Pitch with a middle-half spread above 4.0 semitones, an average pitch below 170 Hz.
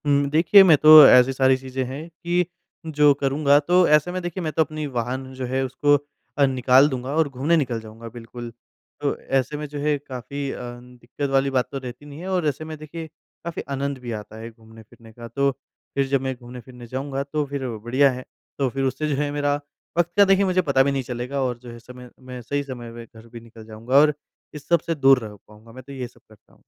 No: average, 3.2 semitones; low, 135 Hz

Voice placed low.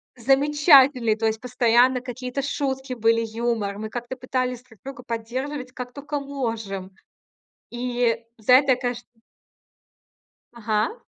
No: high, 245 Hz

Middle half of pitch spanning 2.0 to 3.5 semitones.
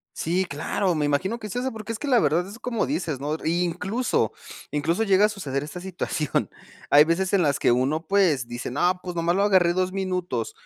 No: average, 4.7 semitones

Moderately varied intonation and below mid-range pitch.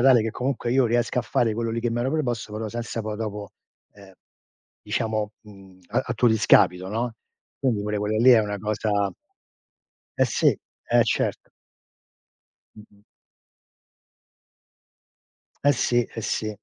No: narrow, 2.3 semitones; low, 110 Hz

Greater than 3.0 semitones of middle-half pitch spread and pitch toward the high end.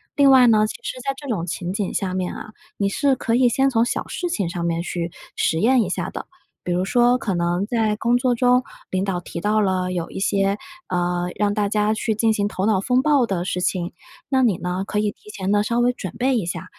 Yes: average, 4.8 semitones; high, 210 Hz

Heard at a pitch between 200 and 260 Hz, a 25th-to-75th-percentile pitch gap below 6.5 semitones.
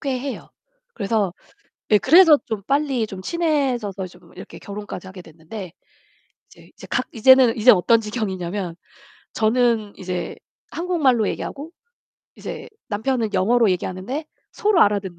Yes: high, 220 Hz; wide, 5.5 semitones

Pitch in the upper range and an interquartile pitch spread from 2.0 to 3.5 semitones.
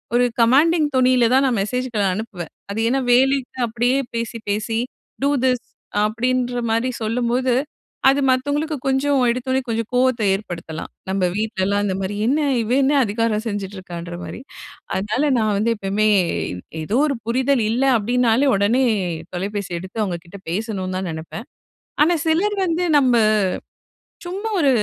No: high, 235 Hz; average, 4.2 semitones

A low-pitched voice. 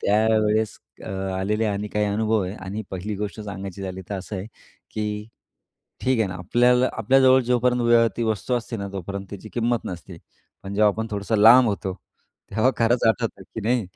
Yes: low, 105 Hz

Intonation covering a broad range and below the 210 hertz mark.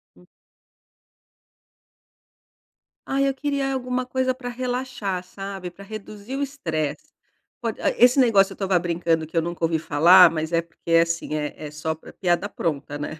Yes: wide, 7.2 semitones; high, 190 Hz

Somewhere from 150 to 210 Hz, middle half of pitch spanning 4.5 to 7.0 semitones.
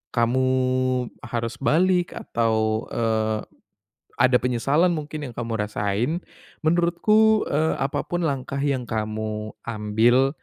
No: low, 125 Hz; wide, 5.6 semitones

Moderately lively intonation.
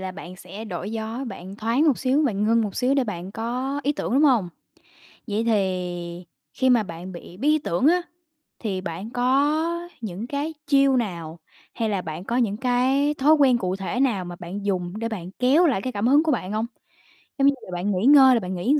No: wide, 6.3 semitones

